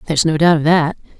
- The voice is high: No, medium, 160 Hz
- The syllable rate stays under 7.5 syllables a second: No, 8.5 syllables/s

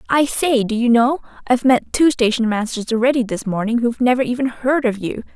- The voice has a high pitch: Yes, high, 240 Hz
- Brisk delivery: Yes, fast, 215 wpm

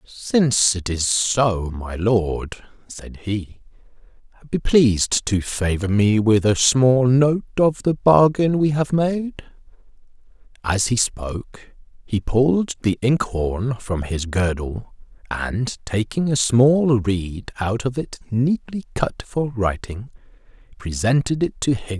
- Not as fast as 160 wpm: Yes, average, 145 wpm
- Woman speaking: No, male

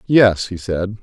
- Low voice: Yes, low, 100 Hz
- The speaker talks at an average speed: Yes, average, 175 wpm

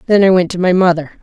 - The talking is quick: Yes, fast, 295 wpm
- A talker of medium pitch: Yes, medium, 180 Hz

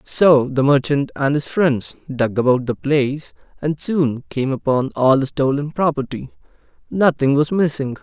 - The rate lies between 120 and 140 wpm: No, average, 155 wpm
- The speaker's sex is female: No, male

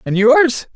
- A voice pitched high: Yes, high, 210 Hz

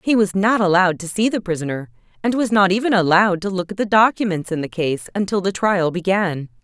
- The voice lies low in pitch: No, high, 190 Hz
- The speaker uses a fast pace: Yes, fast, 215 wpm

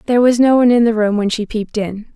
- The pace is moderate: No, fast, 305 wpm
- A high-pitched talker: Yes, high, 225 Hz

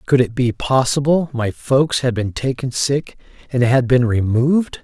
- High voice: No, low, 130 Hz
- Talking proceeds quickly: No, average, 175 wpm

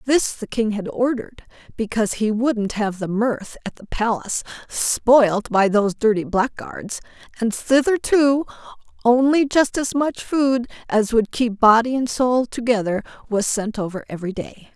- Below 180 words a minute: Yes, average, 155 wpm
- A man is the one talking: No, female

